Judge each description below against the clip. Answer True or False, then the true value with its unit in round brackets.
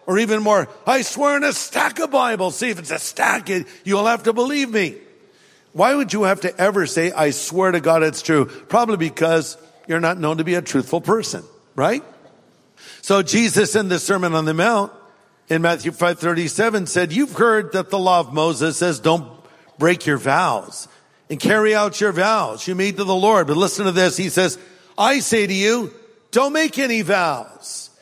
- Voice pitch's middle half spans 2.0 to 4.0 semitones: False (4.8 semitones)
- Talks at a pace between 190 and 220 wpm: True (200 wpm)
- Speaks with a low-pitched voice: False (190 Hz)